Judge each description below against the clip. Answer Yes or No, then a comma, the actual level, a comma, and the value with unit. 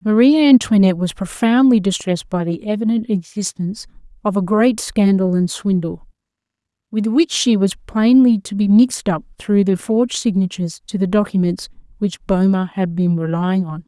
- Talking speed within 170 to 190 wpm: No, average, 160 wpm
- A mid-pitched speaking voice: No, high, 200 Hz